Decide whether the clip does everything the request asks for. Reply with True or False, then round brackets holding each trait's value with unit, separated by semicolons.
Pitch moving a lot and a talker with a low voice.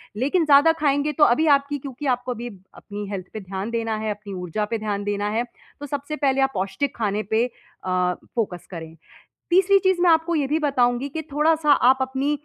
False (5.9 semitones; 255 Hz)